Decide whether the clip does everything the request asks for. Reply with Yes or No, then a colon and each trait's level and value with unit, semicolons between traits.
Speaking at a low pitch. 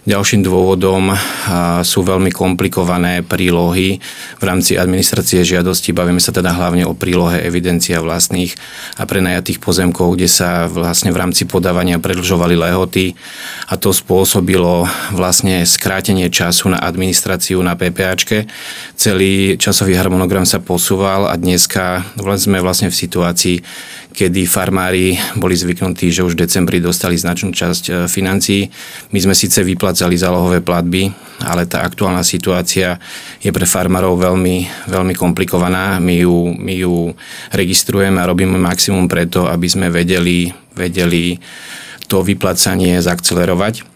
Yes: very low, 90 Hz